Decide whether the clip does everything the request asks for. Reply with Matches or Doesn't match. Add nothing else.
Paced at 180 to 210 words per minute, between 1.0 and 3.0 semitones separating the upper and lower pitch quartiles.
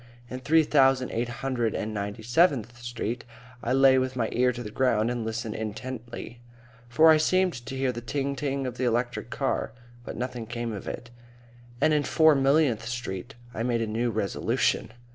Matches